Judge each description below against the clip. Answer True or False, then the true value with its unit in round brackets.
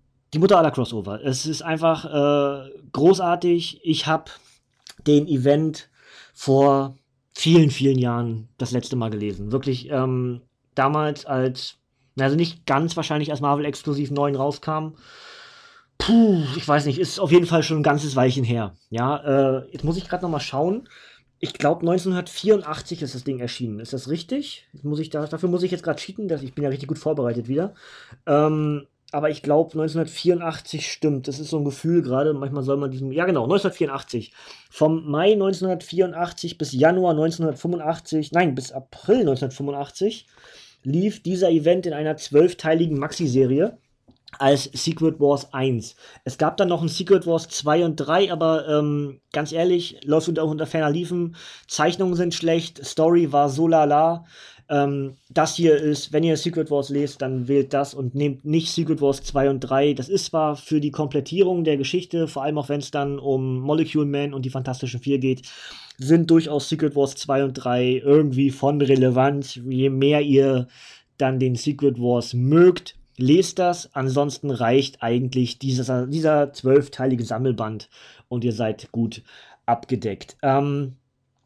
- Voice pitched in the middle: True (145 Hz)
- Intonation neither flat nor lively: True (3.5 semitones)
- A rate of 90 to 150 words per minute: False (165 wpm)